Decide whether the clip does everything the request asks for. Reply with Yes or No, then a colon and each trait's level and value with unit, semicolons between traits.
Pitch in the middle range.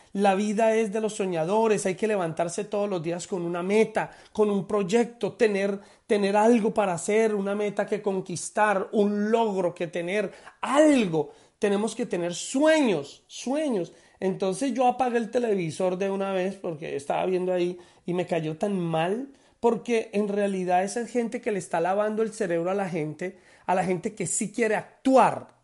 No: high, 205 Hz